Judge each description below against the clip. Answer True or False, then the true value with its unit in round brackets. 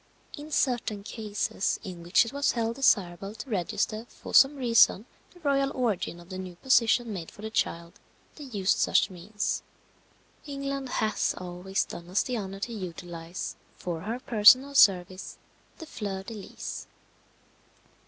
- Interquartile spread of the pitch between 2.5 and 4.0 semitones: False (5.3 semitones)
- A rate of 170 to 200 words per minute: False (155 wpm)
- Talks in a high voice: True (210 Hz)